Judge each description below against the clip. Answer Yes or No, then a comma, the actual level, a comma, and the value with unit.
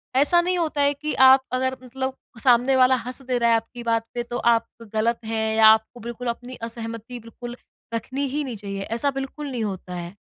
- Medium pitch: No, high, 245 Hz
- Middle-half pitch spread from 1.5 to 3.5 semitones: Yes, average, 2.7 semitones